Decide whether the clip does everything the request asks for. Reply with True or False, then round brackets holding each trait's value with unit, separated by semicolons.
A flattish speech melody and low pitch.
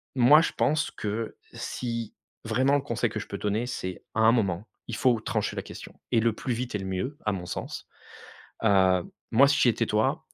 False (3.7 semitones; 115 Hz)